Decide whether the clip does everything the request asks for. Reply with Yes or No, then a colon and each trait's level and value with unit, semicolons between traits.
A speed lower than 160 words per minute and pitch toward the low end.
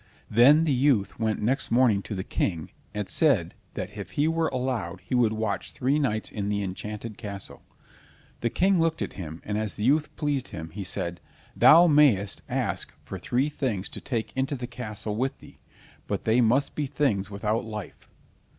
No: average, 185 wpm; low, 115 Hz